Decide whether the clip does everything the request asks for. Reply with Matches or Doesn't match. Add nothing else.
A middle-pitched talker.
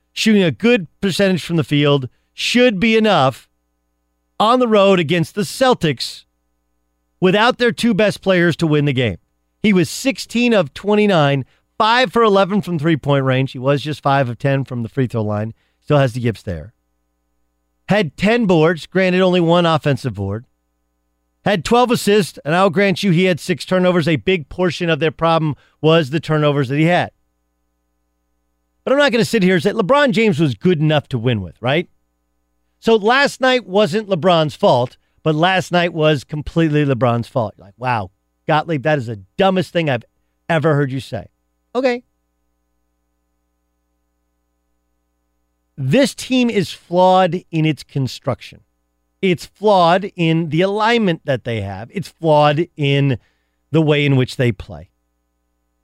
Matches